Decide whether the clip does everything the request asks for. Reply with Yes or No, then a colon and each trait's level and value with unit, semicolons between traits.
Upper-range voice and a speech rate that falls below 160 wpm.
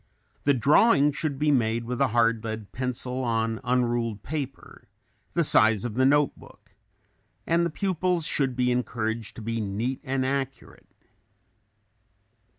No: low, 125 Hz; average, 150 wpm